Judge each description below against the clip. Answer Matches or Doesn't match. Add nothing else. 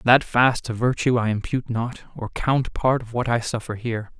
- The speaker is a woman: Doesn't match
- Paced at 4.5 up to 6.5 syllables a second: Matches